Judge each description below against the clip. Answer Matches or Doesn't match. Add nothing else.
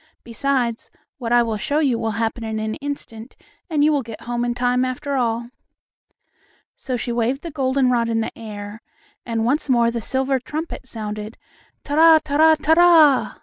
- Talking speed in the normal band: Matches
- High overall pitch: Matches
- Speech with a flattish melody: Doesn't match